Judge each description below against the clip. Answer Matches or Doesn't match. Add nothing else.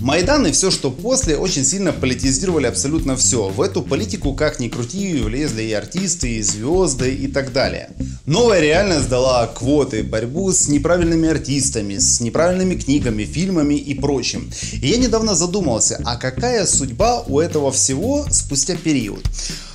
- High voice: Doesn't match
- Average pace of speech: Matches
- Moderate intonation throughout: Doesn't match